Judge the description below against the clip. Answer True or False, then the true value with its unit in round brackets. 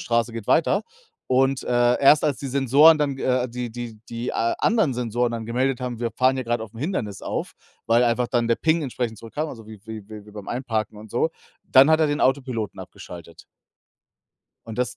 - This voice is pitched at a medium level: False (120 Hz)